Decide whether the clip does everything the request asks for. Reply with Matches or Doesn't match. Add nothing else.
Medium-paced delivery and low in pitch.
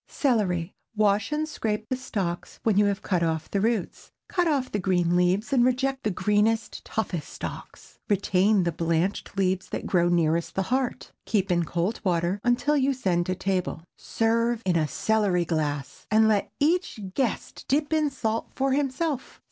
Doesn't match